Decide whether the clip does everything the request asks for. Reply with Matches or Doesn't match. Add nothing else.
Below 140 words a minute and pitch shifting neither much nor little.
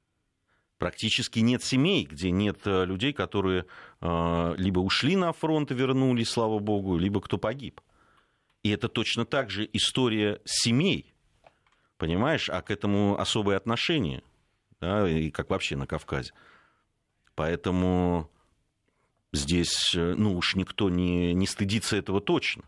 Matches